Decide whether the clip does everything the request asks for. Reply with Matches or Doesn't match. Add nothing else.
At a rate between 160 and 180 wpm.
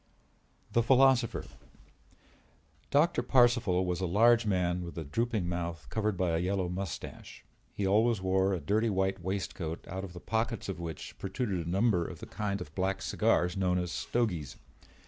Matches